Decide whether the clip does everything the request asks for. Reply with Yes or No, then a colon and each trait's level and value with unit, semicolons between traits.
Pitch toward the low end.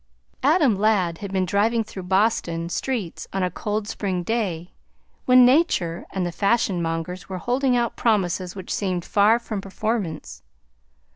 No: high, 200 Hz